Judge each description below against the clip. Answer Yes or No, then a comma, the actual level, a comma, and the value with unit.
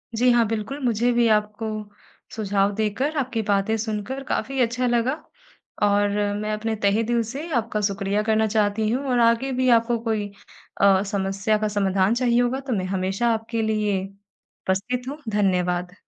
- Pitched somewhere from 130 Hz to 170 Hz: No, high, 220 Hz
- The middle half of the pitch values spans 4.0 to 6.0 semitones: No, average, 2.9 semitones